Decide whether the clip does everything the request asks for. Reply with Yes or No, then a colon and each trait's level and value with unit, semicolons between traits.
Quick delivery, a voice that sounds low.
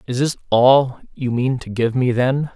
Yes: fast, 210 wpm; low, 125 Hz